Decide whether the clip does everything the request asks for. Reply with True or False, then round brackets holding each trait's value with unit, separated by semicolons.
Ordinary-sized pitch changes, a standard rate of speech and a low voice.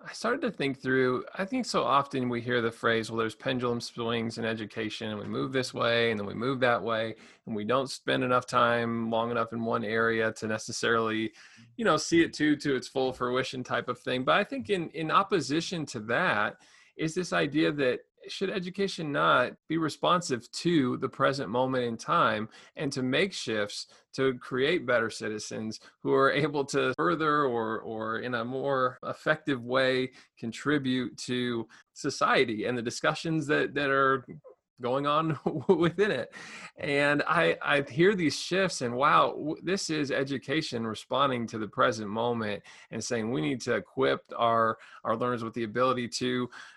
True (4.4 semitones; 180 wpm; 130 Hz)